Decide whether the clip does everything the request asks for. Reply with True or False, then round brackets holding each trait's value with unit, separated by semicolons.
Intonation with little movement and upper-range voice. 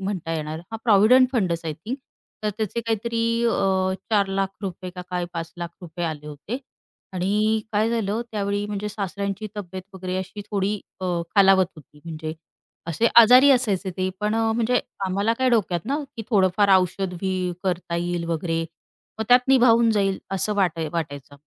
False (3.7 semitones; 195 Hz)